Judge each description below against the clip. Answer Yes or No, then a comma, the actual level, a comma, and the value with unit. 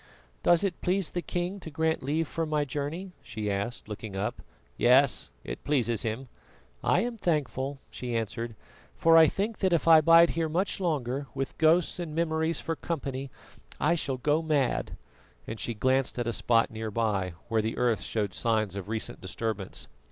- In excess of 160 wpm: Yes, average, 180 wpm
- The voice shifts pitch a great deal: Yes, wide, 6.4 semitones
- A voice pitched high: No, medium, 140 Hz